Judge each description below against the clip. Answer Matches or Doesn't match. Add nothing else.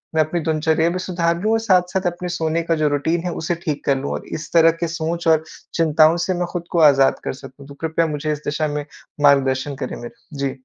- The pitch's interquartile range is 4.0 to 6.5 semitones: Doesn't match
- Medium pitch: Matches